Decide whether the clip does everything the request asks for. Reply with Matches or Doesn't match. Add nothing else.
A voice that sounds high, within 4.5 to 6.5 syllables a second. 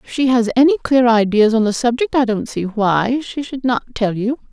Matches